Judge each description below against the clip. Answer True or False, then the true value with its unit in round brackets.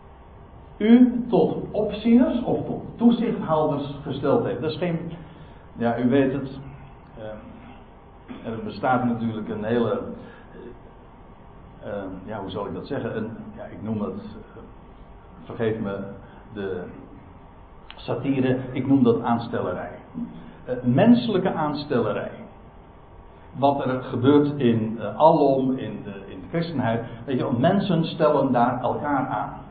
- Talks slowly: True (130 wpm)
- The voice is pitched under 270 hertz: True (135 Hz)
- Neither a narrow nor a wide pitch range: False (5.7 semitones)